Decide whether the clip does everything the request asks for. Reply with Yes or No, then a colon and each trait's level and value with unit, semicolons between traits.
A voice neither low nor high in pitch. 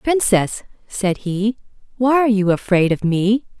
No: high, 210 Hz